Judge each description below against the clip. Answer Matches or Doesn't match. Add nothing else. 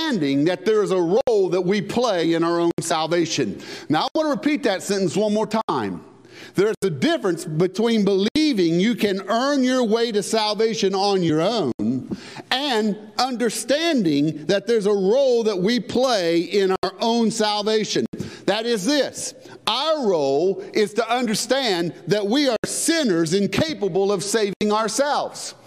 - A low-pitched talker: Doesn't match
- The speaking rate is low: Doesn't match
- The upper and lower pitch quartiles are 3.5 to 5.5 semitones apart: Matches